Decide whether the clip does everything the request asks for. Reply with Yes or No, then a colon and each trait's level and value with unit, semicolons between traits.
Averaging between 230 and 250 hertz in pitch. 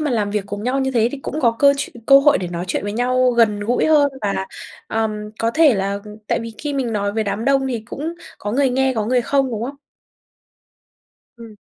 Yes: high, 235 Hz